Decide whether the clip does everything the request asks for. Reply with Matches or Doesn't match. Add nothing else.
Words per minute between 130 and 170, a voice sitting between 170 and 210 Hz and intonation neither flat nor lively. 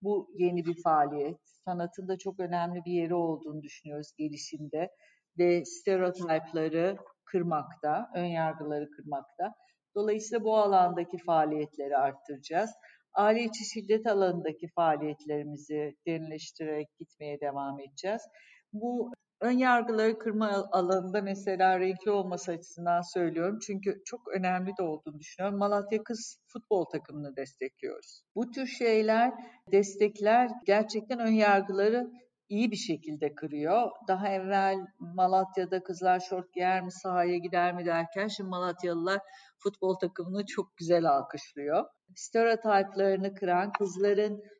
Doesn't match